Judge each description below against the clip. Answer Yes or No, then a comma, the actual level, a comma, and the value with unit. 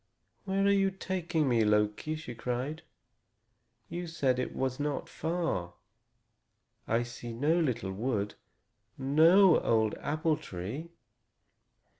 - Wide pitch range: Yes, wide, 6.3 semitones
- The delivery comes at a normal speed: No, slow, 115 wpm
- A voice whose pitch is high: No, medium, 140 Hz